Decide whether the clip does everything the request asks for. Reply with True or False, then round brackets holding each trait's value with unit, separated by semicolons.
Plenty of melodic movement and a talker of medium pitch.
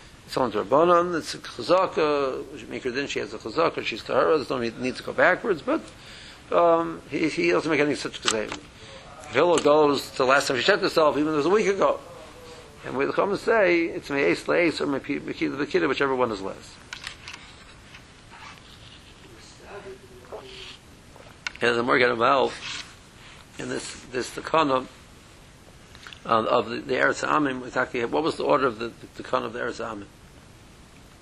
True (7.3 semitones; 150 Hz)